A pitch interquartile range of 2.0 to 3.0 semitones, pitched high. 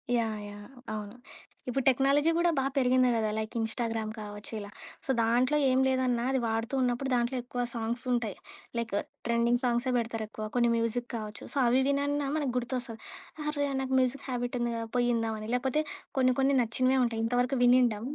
Yes: narrow, 2.4 semitones; high, 245 Hz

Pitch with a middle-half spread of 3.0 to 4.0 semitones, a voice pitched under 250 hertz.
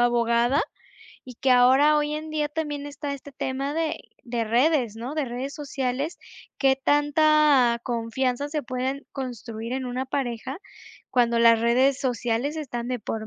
No: average, 3.3 semitones; very high, 260 Hz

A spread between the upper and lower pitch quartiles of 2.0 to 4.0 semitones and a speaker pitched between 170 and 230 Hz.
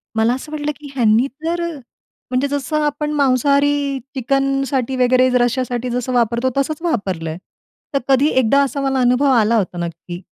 No: average, 2.7 semitones; very high, 260 Hz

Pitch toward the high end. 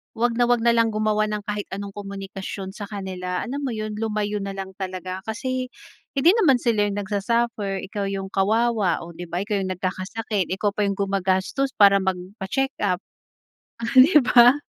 Yes: high, 205 Hz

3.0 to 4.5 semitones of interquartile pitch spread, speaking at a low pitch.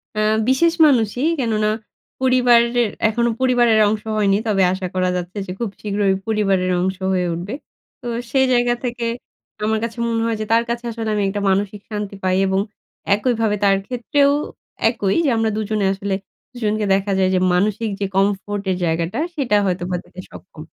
No: average, 3.4 semitones; high, 215 Hz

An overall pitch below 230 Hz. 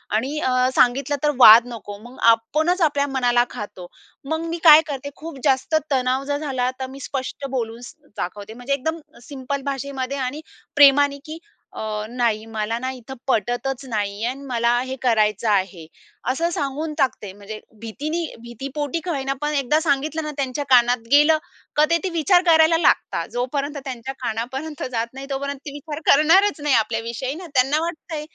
No: very high, 270 Hz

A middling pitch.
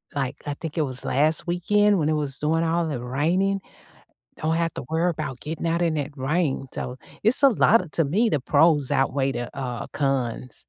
Yes: medium, 155 Hz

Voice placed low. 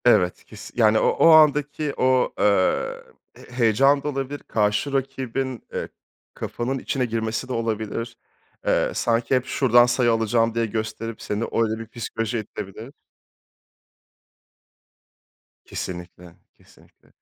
Yes: low, 115 Hz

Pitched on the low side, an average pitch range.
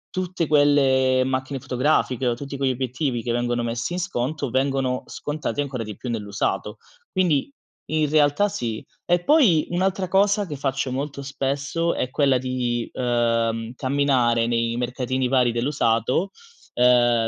Yes: low, 130 Hz; average, 3.3 semitones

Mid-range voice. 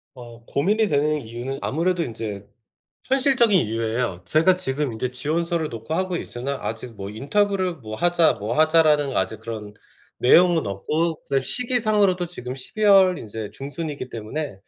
Yes: medium, 145 Hz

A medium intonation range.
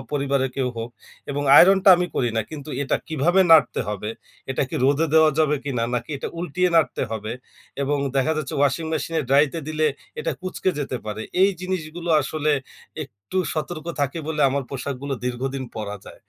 Yes: average, 3.3 semitones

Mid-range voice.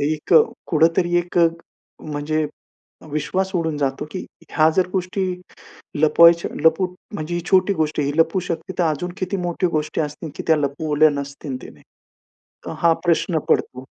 Yes: medium, 160 Hz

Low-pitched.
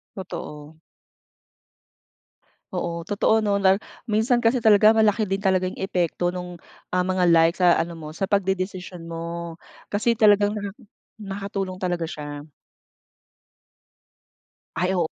No: medium, 185 Hz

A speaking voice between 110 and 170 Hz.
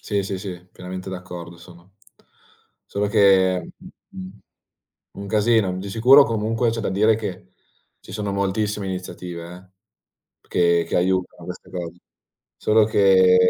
No: very low, 95 Hz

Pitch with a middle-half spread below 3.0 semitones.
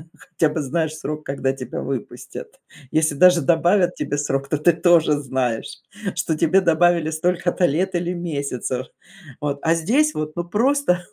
No: average, 3.4 semitones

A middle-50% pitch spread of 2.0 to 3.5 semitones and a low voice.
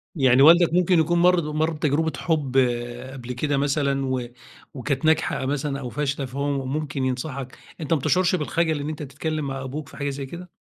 No: average, 2.9 semitones; medium, 145 Hz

